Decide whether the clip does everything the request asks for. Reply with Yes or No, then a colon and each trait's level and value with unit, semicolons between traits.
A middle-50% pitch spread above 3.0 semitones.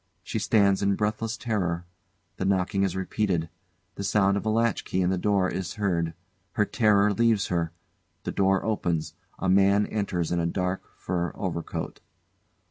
No: average, 2.7 semitones